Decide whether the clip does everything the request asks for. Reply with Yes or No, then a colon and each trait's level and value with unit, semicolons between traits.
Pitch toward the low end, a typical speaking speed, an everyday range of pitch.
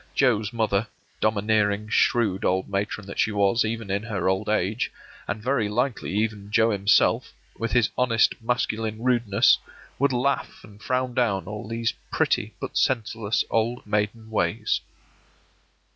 No: low, 110 Hz; average, 145 wpm; narrow, 2.3 semitones